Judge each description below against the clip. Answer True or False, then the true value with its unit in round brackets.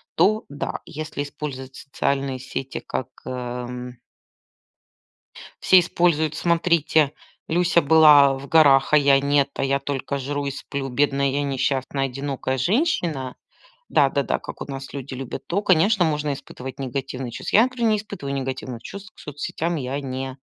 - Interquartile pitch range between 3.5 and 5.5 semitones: False (2.9 semitones)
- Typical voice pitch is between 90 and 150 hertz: True (140 Hz)